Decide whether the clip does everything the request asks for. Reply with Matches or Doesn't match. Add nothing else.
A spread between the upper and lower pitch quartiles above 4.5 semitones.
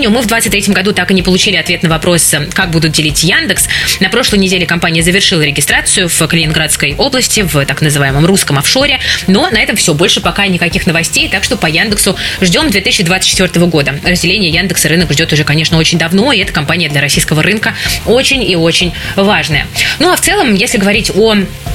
Doesn't match